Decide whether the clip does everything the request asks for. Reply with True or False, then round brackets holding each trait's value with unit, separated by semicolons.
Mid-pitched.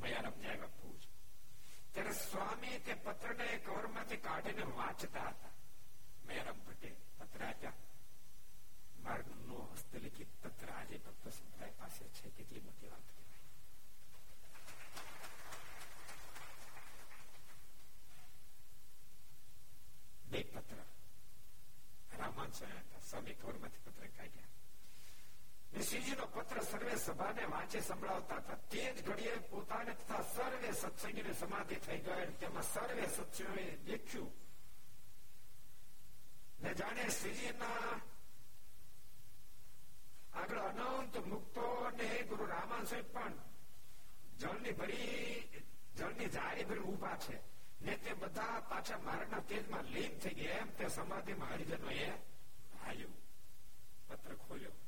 False (230 Hz)